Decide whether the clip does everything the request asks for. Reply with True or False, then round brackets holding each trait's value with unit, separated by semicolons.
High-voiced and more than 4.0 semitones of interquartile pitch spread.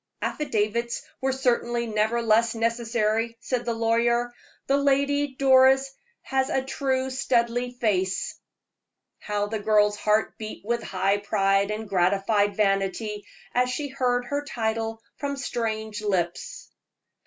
False (230 Hz; 3.4 semitones)